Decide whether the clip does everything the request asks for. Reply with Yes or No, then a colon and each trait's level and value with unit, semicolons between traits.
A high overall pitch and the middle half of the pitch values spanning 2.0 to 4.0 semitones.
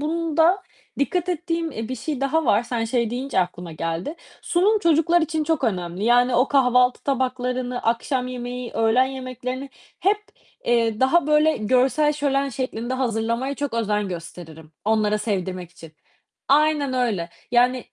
No: very high, 250 Hz; average, 4.7 semitones